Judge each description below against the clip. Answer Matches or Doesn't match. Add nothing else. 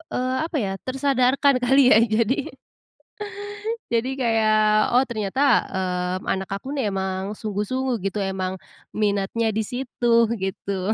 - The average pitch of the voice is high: Matches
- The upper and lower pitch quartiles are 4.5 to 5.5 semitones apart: Matches